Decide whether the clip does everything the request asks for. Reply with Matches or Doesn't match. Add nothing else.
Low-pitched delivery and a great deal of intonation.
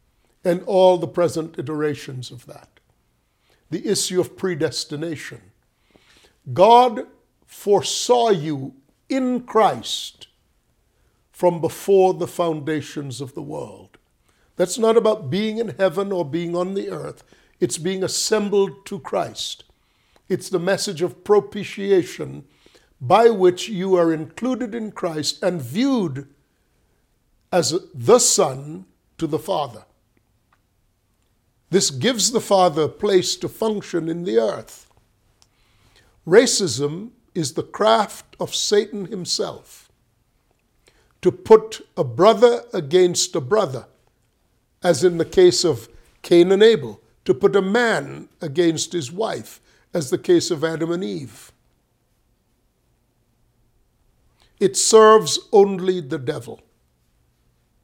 Doesn't match